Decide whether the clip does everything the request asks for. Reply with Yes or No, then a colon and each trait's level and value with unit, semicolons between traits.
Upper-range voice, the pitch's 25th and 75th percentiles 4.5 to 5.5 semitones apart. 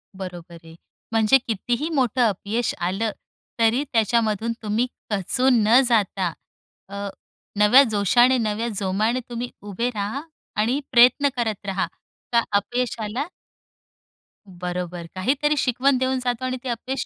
No: high, 225 Hz; average, 3.8 semitones